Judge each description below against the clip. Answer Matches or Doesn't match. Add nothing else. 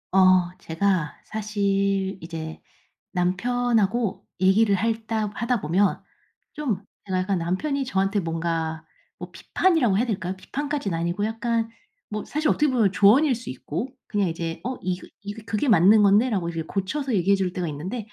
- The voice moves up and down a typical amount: Matches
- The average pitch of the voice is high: Matches